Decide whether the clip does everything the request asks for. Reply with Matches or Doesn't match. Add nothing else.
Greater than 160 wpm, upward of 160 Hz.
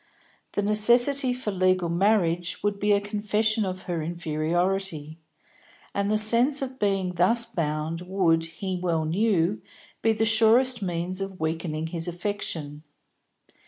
Doesn't match